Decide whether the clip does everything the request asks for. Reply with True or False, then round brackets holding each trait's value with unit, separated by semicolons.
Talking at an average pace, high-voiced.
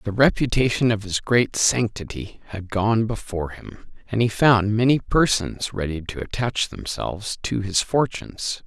False (150 wpm; 110 Hz)